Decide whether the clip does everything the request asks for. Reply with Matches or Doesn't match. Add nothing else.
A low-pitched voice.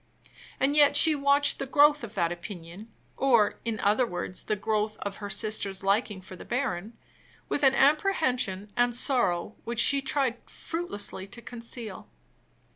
Doesn't match